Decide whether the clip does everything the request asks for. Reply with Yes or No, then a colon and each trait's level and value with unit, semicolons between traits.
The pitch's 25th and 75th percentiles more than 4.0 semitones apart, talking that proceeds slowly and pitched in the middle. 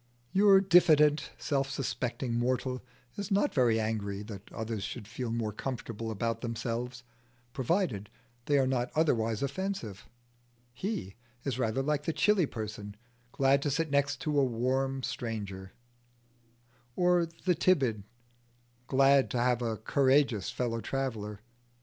No: average, 4.4 semitones; slow, 130 wpm; low, 130 Hz